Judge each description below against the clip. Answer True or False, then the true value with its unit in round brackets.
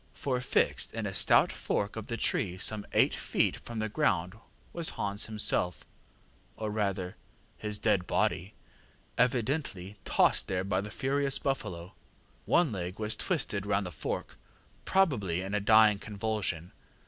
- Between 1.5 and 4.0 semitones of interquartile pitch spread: True (3.2 semitones)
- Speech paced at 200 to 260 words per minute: False (150 wpm)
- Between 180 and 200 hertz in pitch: False (105 Hz)